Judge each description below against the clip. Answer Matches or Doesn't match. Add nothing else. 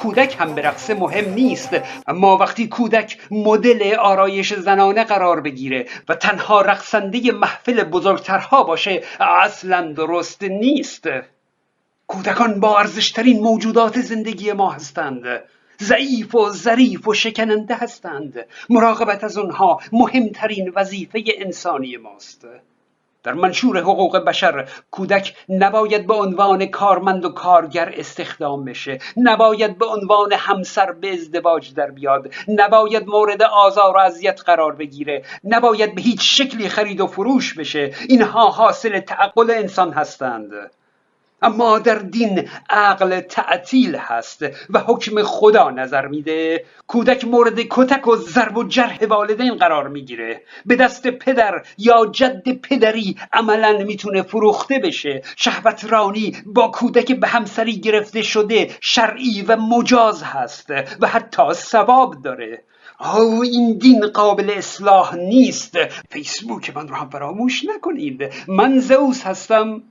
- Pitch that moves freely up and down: Doesn't match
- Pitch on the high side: Matches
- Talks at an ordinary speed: Matches